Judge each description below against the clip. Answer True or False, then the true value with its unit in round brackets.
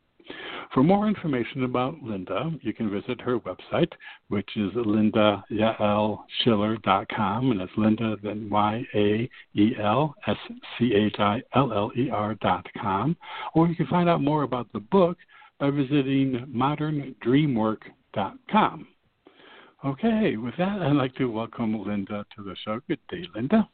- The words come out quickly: False (145 wpm)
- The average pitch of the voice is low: True (120 Hz)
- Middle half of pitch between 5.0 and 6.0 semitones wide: True (5.4 semitones)